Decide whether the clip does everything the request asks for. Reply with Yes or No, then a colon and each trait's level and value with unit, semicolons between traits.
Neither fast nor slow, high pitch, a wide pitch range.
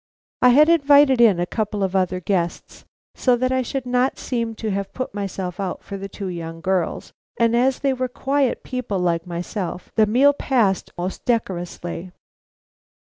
Yes: average, 170 wpm; high, 210 Hz; wide, 5.7 semitones